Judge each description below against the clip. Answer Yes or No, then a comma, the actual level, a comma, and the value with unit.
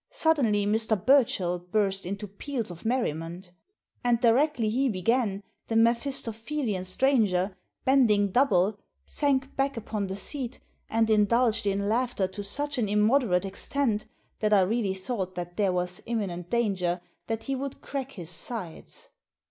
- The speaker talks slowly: No, average, 145 wpm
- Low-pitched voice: No, high, 215 Hz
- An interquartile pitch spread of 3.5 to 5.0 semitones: Yes, average, 4.6 semitones